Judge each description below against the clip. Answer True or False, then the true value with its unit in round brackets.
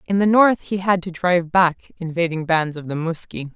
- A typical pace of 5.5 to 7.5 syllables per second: False (5.2 syllables/s)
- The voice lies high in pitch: False (175 Hz)